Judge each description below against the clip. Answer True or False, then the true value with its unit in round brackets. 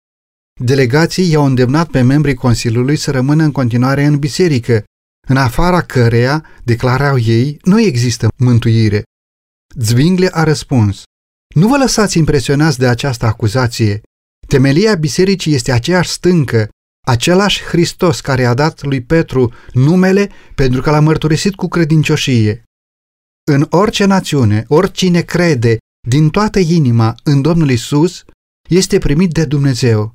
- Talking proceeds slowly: False (125 wpm)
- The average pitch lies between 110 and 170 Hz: True (140 Hz)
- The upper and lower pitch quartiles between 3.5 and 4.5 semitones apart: False (5.6 semitones)